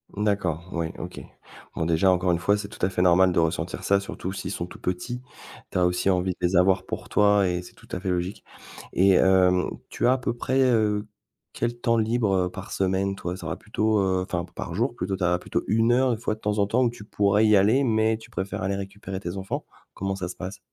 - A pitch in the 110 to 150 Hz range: No, very low, 95 Hz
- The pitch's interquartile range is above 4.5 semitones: No, average, 2.9 semitones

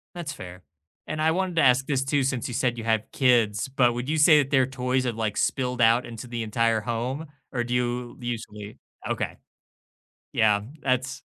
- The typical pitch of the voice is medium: No, low, 125 Hz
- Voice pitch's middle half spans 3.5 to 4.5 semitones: No, average, 2.7 semitones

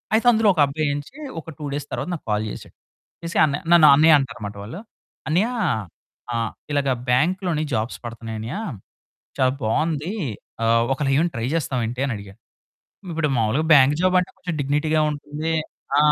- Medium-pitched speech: Yes, medium, 145 Hz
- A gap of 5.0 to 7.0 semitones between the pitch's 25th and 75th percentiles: Yes, wide, 5.4 semitones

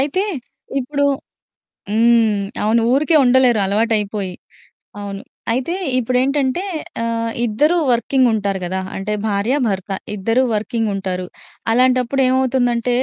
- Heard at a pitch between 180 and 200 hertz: No, high, 230 Hz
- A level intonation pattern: No, average, 3.8 semitones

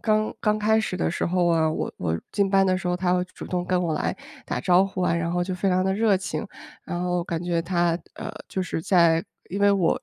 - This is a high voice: No, medium, 180 Hz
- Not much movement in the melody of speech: Yes, narrow, 2.1 semitones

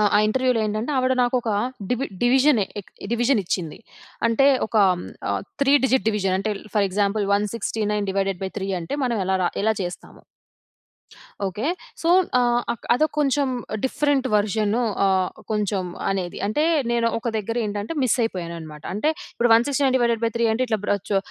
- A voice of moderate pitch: No, high, 220 Hz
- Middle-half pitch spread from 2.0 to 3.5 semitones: No, average, 3.9 semitones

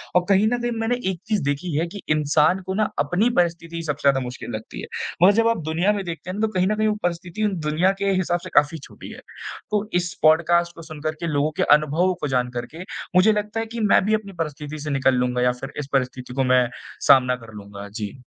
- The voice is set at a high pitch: No, medium, 165 Hz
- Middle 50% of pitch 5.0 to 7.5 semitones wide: Yes, wide, 5.5 semitones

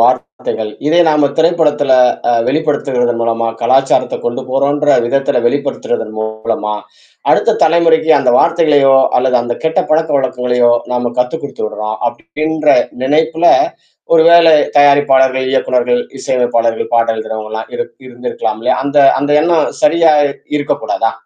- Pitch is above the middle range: No, low, 135 Hz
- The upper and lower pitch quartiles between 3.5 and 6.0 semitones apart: Yes, average, 4.3 semitones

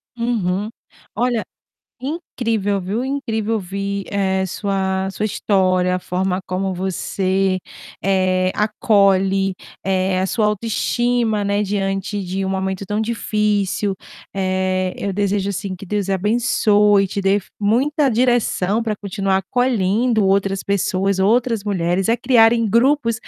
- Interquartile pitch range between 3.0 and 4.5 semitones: No, narrow, 2.6 semitones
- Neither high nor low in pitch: No, high, 200 Hz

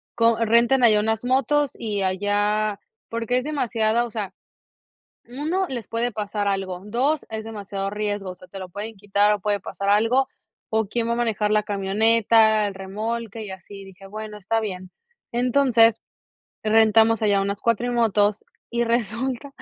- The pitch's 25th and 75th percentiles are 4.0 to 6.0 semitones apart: No, narrow, 2.4 semitones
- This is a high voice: Yes, high, 220 Hz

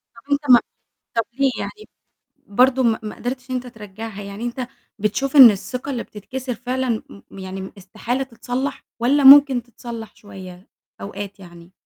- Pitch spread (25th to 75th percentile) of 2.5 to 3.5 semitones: No, average, 4.2 semitones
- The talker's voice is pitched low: No, high, 240 Hz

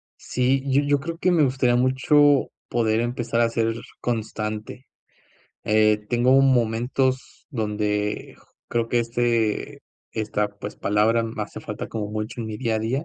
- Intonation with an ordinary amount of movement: Yes, average, 3.1 semitones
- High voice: No, low, 115 Hz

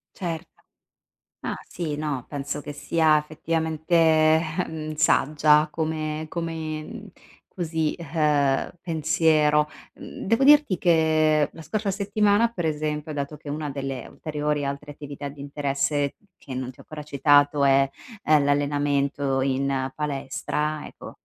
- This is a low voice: No, medium, 150 Hz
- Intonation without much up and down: Yes, narrow, 2.0 semitones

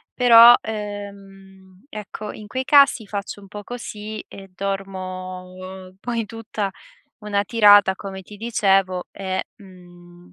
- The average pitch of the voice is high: Yes, high, 200 Hz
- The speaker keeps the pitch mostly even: Yes, narrow, 2.2 semitones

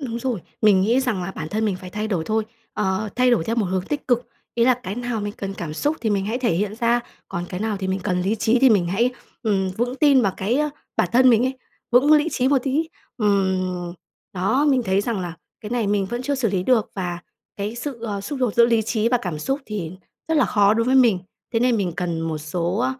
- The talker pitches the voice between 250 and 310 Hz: No, high, 215 Hz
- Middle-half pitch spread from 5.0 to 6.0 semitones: No, average, 4.5 semitones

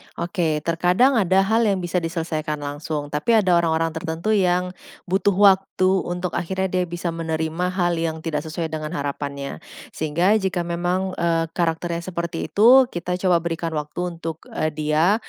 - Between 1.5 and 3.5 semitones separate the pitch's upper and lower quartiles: Yes, narrow, 2.4 semitones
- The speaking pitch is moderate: Yes, medium, 170 Hz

